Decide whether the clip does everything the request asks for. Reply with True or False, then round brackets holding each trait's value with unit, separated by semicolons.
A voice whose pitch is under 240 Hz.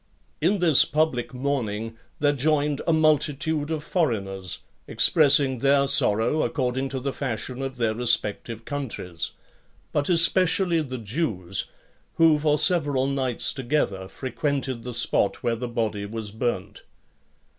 True (135 Hz)